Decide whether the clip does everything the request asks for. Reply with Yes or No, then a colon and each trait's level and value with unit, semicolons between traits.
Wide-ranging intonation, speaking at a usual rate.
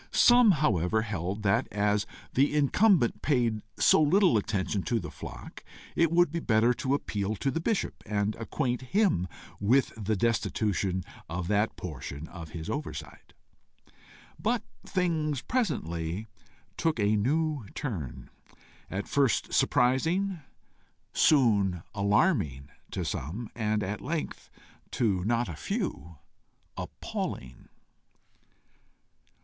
No: wide, 7.5 semitones; slow, 115 wpm